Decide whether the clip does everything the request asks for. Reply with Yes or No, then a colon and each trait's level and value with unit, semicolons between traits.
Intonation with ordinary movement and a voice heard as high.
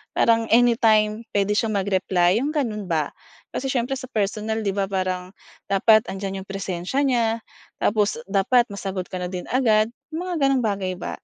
Yes: average, 3.4 semitones; high, 210 Hz